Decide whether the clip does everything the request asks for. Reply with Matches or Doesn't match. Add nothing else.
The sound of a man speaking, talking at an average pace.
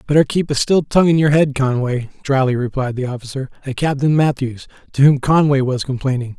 Matches